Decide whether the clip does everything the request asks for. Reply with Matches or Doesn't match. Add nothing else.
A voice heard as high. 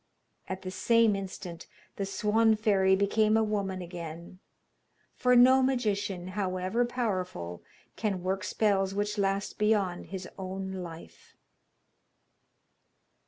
Matches